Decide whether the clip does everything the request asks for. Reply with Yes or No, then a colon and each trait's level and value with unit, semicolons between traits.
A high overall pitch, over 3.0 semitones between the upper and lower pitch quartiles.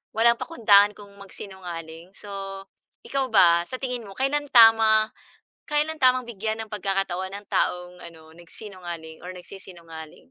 Yes: high, 200 Hz; average, 4.3 semitones